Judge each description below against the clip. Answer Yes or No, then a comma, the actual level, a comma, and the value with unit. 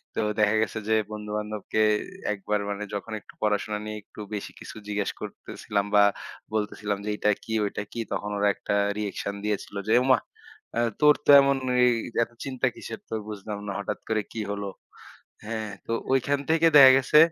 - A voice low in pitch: Yes, low, 105 Hz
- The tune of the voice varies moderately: No, narrow, 2.0 semitones